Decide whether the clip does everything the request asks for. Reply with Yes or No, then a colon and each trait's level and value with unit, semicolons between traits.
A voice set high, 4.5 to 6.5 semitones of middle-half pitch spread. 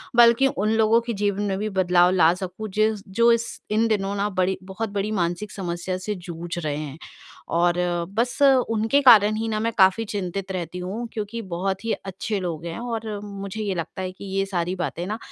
No: high, 200 Hz; average, 3.2 semitones